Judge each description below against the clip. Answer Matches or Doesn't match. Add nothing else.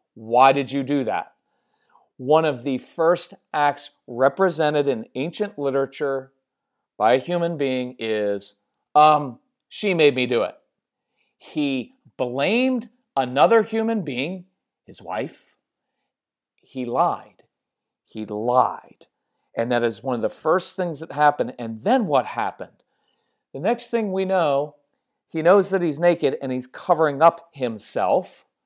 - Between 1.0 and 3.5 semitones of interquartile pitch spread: Doesn't match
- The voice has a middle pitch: Matches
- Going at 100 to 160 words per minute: Matches